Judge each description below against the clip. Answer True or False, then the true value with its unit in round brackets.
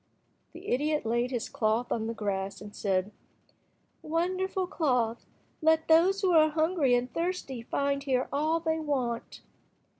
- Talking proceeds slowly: False (145 wpm)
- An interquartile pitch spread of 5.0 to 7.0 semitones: True (5.5 semitones)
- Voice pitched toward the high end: True (280 Hz)